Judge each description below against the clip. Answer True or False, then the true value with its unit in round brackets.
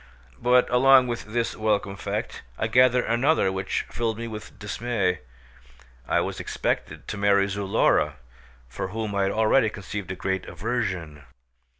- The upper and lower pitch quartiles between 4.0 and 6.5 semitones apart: False (3.4 semitones)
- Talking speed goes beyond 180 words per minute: False (150 wpm)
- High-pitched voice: False (110 Hz)